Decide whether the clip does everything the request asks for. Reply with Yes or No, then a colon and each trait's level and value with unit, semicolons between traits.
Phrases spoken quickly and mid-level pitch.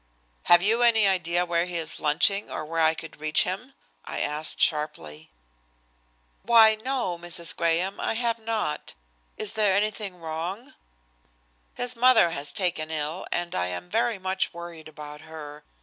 No: average, 160 wpm; medium, 170 Hz